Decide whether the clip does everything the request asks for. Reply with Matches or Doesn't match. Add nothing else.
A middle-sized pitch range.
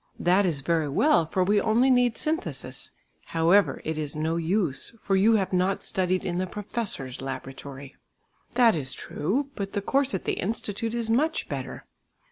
Doesn't match